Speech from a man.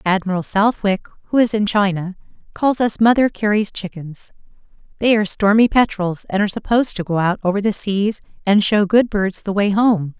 No: female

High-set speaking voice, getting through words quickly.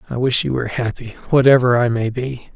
No: low, 125 Hz; fast, 210 wpm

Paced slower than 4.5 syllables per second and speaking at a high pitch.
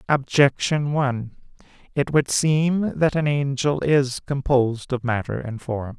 No: 4.1 syllables/s; low, 135 Hz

